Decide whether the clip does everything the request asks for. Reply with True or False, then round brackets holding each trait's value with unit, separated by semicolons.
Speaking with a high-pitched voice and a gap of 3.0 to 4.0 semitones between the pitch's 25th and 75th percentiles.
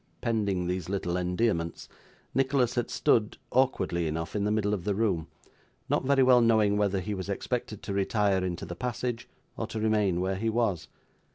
False (105 Hz; 3.7 semitones)